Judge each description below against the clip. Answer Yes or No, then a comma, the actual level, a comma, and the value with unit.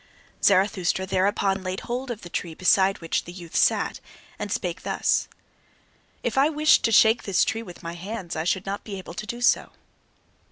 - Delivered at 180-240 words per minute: Yes, average, 190 wpm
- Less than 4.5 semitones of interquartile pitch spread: Yes, average, 3.8 semitones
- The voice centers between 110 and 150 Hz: No, high, 195 Hz